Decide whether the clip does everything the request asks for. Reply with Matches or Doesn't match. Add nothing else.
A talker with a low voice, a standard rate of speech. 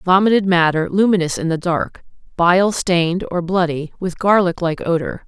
Doesn't match